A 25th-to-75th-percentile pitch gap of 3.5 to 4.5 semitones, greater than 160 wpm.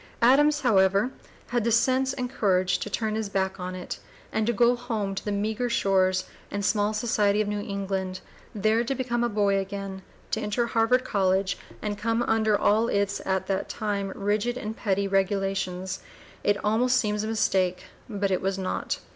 No: average, 2.9 semitones; average, 180 wpm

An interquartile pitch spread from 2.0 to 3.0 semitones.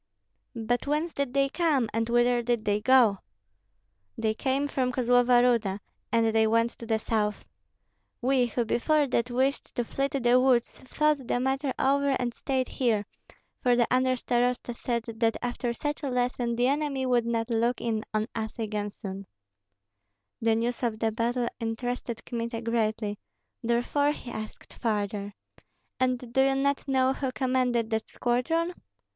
Yes: narrow, 2.5 semitones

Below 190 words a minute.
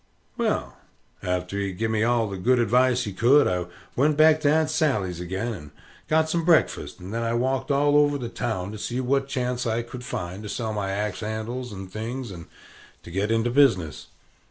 No: fast, 205 wpm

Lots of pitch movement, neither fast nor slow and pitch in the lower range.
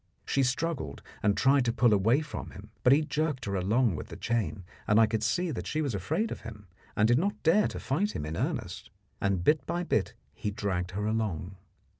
No: wide, 6.5 semitones; fast, 220 wpm; low, 115 Hz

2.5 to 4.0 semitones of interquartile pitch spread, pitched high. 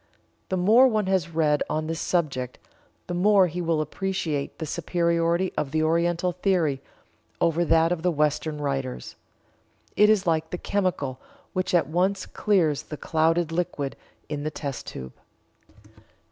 No: average, 3.0 semitones; medium, 165 Hz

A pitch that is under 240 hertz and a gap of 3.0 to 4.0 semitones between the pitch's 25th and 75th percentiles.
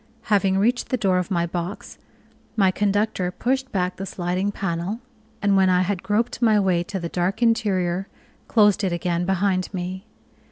No: high, 190 Hz; narrow, 2.4 semitones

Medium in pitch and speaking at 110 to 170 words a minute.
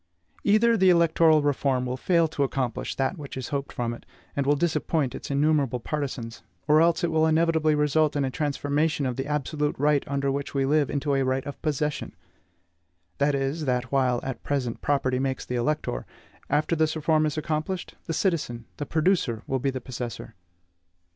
No: medium, 145 Hz; average, 185 wpm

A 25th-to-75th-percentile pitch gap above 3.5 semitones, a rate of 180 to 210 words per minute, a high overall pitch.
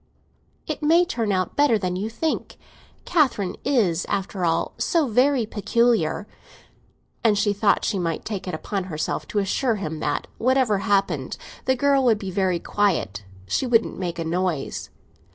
No: average, 4.9 semitones; average, 155 wpm; high, 205 Hz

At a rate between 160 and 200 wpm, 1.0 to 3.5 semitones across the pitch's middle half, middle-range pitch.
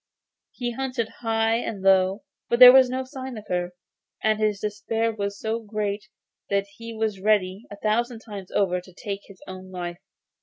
No: average, 180 wpm; average, 2.8 semitones; high, 215 Hz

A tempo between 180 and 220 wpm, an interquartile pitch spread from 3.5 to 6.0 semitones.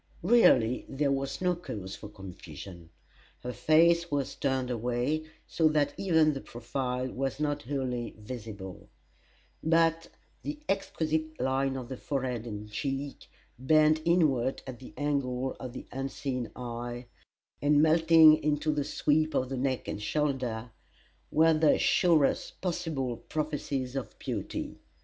No: slow, 135 wpm; average, 3.8 semitones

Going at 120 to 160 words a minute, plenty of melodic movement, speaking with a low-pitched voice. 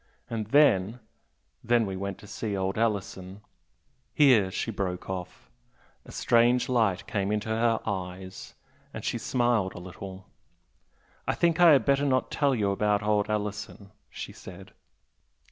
No: average, 150 wpm; average, 3.6 semitones; low, 105 Hz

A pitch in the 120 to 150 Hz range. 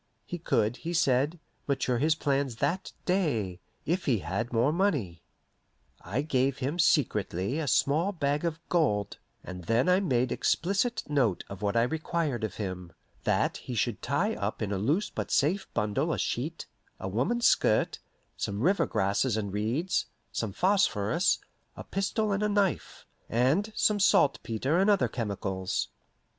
Yes: low, 135 Hz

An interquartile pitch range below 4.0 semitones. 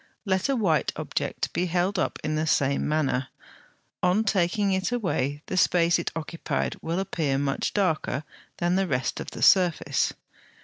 Yes: average, 3.5 semitones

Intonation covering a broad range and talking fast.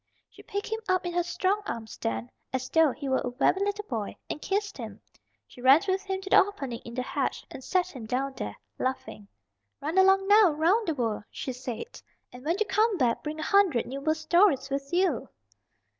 Yes: wide, 7.0 semitones; fast, 215 wpm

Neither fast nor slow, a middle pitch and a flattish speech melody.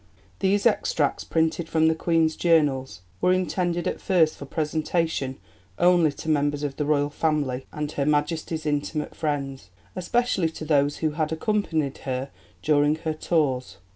Yes: average, 150 wpm; medium, 155 Hz; narrow, 2.3 semitones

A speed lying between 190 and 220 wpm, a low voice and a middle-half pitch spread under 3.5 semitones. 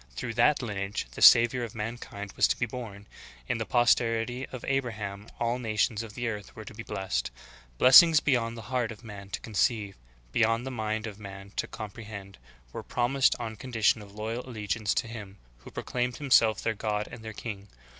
Yes: average, 195 wpm; low, 110 Hz; average, 2.7 semitones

